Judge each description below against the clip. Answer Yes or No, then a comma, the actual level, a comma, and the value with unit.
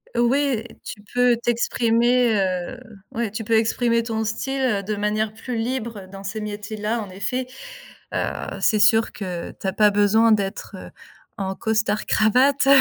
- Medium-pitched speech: No, high, 220 Hz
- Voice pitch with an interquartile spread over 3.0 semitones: No, narrow, 2.4 semitones